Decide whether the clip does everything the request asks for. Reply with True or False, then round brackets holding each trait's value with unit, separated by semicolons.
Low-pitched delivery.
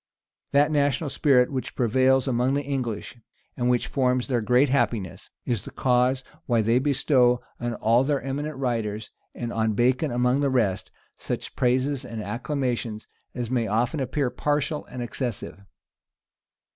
True (125 Hz)